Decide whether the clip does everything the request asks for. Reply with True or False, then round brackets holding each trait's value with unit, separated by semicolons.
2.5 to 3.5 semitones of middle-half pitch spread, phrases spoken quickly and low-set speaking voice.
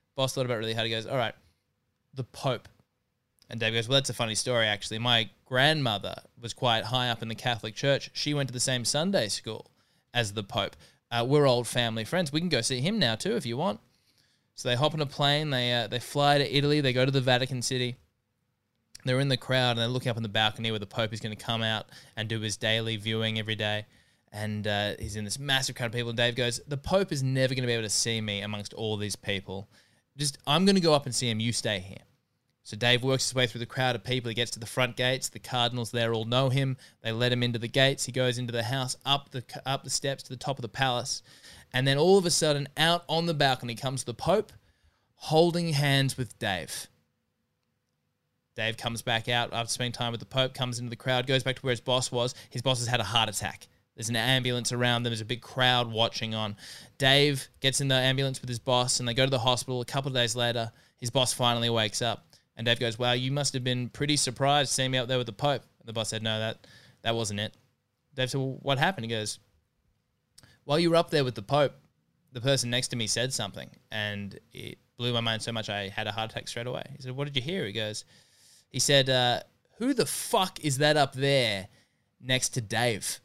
True (2.8 semitones; 250 wpm; 125 Hz)